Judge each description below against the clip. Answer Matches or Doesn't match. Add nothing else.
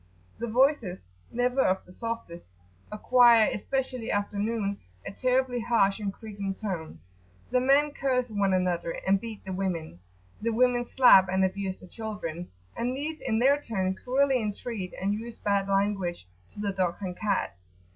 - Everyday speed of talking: Matches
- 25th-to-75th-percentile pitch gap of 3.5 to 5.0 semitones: Matches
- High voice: Matches